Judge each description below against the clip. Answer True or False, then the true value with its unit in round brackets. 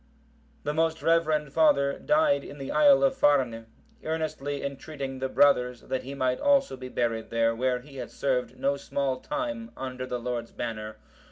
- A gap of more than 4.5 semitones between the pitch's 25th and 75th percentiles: False (3.9 semitones)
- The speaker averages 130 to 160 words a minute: False (170 wpm)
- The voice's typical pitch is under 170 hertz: True (140 Hz)